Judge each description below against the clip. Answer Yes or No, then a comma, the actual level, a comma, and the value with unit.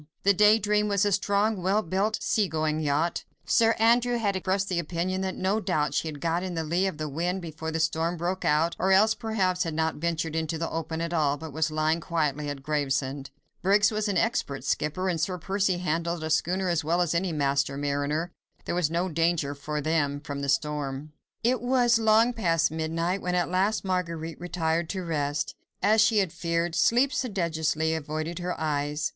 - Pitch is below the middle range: No, medium, 170 Hz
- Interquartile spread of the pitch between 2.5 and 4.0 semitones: Yes, average, 3.7 semitones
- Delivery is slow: No, average, 200 wpm